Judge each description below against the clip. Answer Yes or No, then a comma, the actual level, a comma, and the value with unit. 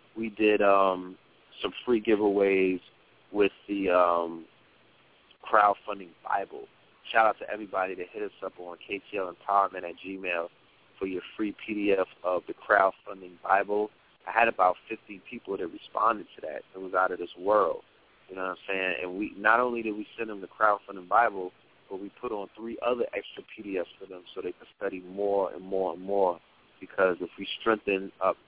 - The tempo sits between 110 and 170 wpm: No, average, 185 wpm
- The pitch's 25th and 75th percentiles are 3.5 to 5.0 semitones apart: No, narrow, 2.5 semitones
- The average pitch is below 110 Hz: Yes, low, 100 Hz